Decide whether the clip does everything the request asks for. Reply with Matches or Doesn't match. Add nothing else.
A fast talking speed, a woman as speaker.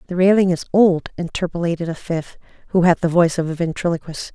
Doesn't match